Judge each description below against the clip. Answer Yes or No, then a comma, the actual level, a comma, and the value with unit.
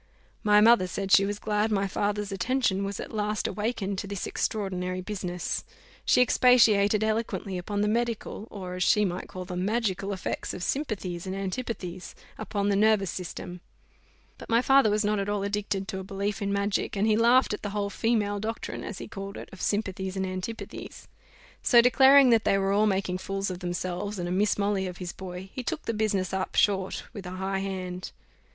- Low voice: No, high, 200 Hz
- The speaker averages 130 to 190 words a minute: No, average, 200 wpm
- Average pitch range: No, narrow, 2.2 semitones